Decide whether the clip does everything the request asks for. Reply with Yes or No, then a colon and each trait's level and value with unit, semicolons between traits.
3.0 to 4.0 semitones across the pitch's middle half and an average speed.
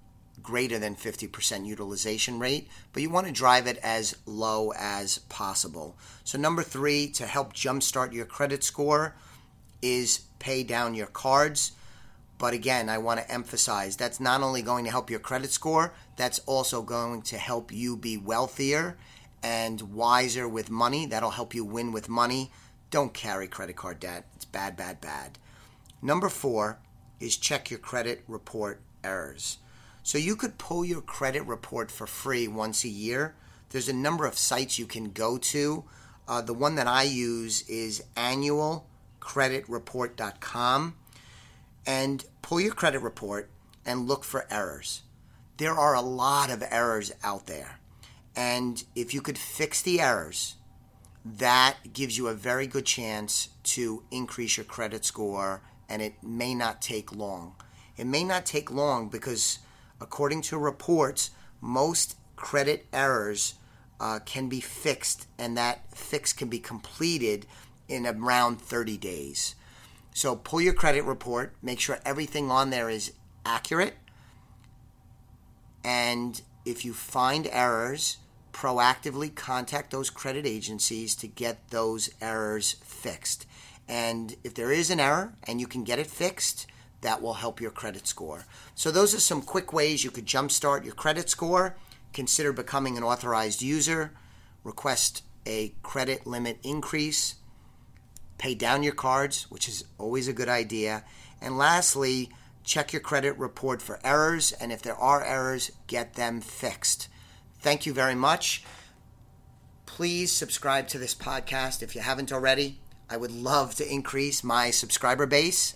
Yes: average, 3.4 semitones; average, 150 wpm